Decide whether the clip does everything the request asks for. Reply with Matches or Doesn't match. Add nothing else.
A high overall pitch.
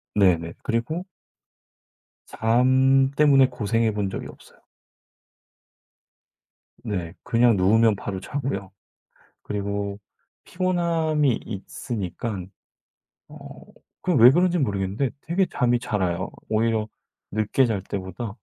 Doesn't match